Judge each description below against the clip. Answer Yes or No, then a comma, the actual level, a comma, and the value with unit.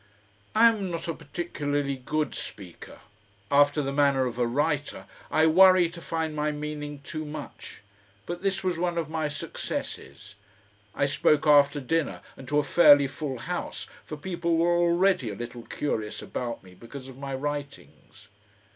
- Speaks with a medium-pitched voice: Yes, medium, 150 Hz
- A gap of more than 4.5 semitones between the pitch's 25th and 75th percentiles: No, average, 3.3 semitones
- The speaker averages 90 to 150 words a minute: No, average, 165 wpm